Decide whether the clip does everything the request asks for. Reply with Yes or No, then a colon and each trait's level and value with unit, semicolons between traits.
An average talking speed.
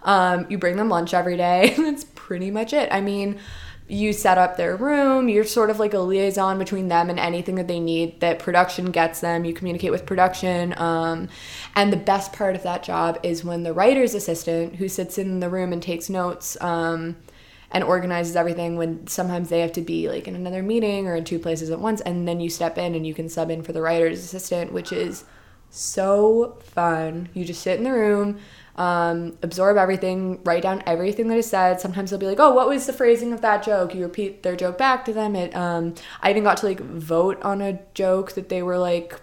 No: fast, 225 wpm